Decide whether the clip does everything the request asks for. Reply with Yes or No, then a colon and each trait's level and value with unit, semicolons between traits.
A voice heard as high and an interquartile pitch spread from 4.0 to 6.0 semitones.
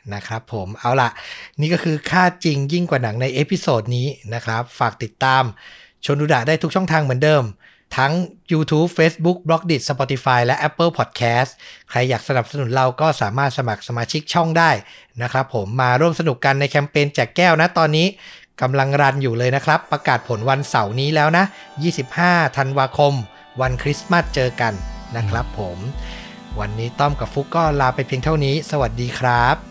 No: medium, 140 Hz; average, 4.3 semitones